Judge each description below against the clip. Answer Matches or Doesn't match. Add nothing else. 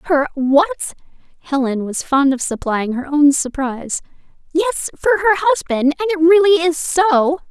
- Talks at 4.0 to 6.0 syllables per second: Doesn't match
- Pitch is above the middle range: Matches